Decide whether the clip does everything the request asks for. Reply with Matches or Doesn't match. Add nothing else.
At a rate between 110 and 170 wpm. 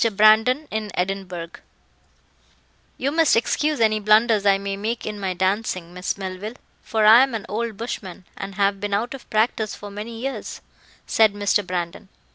Matches